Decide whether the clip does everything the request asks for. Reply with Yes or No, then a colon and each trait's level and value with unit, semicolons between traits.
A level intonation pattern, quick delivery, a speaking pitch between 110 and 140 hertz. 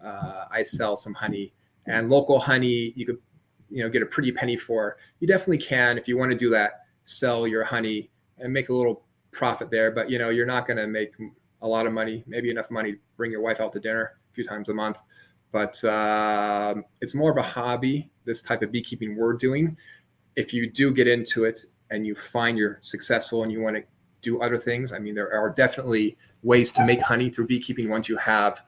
Yes: narrow, 2.3 semitones; fast, 225 wpm; low, 115 Hz